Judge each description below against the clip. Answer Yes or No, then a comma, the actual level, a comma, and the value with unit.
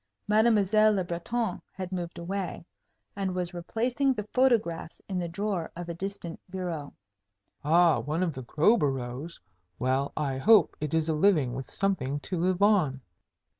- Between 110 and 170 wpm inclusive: Yes, average, 150 wpm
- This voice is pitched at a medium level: Yes, medium, 175 Hz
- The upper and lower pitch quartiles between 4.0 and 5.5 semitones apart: Yes, average, 4.4 semitones